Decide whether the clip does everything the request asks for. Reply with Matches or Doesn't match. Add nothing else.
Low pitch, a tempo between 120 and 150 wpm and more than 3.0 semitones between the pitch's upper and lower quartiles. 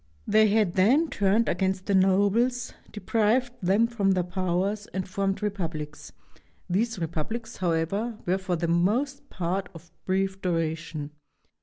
Doesn't match